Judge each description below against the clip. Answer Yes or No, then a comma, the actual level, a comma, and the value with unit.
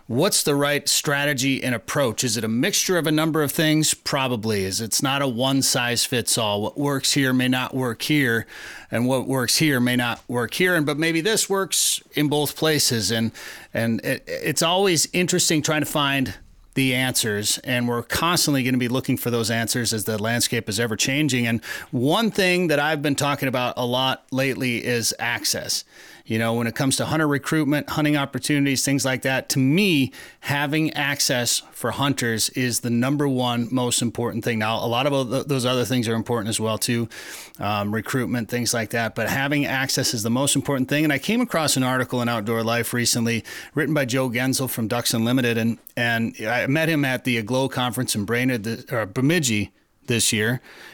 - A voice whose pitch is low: Yes, low, 130 Hz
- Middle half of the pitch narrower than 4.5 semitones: Yes, average, 3.5 semitones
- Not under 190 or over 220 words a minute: Yes, average, 200 wpm